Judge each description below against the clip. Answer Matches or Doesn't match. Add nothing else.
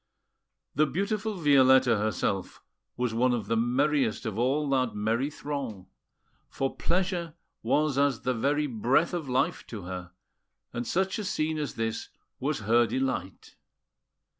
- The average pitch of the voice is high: Doesn't match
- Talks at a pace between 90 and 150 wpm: Matches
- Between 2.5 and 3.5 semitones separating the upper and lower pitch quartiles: Doesn't match